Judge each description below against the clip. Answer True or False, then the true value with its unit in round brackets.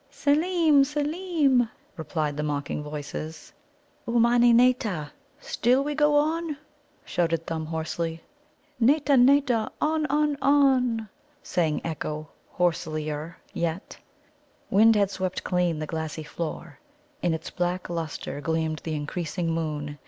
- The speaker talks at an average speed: False (115 wpm)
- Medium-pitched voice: True (180 Hz)